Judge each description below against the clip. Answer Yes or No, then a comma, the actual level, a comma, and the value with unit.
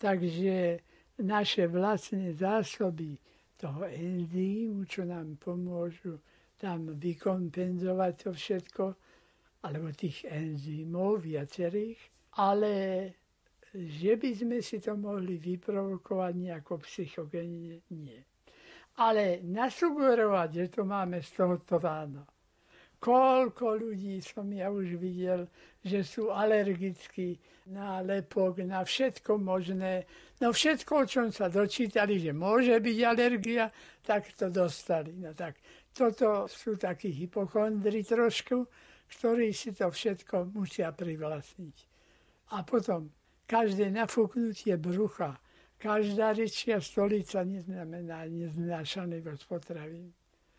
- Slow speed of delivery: Yes, slow, 100 wpm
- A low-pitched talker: No, high, 190 Hz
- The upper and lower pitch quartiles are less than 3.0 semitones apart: No, average, 3.6 semitones